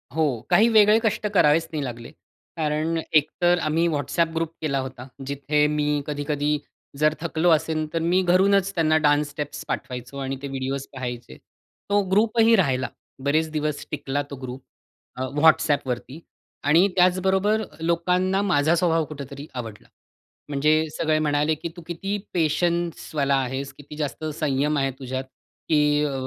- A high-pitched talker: No, medium, 150 Hz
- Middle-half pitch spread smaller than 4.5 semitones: Yes, average, 3.3 semitones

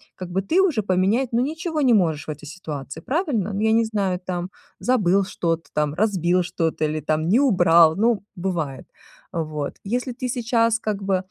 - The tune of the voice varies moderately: No, wide, 5.7 semitones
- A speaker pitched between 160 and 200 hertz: Yes, high, 190 Hz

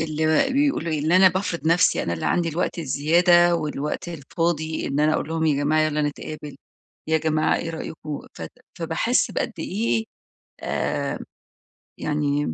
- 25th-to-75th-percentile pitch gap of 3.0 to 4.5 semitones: No, narrow, 2.4 semitones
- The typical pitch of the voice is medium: Yes, medium, 155 Hz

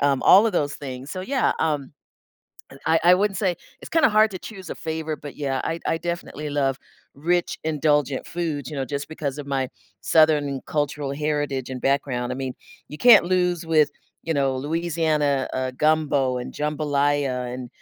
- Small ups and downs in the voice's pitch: No, average, 3.1 semitones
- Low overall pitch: No, medium, 150 Hz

